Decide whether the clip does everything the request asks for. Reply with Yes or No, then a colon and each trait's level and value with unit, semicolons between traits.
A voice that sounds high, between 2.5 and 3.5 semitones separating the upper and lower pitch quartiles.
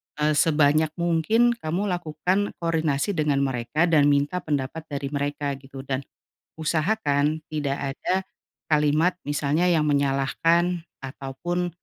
No: medium, 150 Hz; average, 2.9 semitones